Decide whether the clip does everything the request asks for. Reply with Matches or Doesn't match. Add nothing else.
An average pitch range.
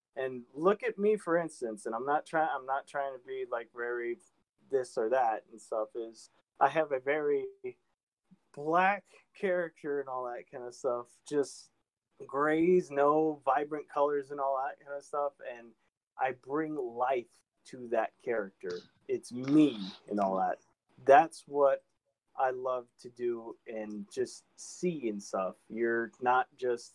Doesn't match